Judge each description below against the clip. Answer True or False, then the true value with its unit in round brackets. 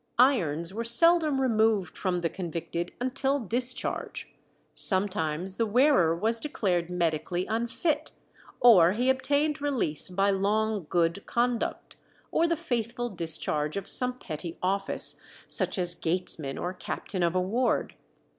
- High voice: True (200 Hz)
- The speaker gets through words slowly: True (130 wpm)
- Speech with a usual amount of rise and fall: False (6.1 semitones)